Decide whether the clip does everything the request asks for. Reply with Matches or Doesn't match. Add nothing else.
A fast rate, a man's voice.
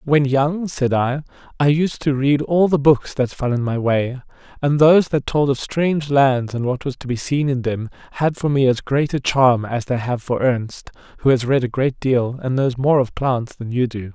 Matches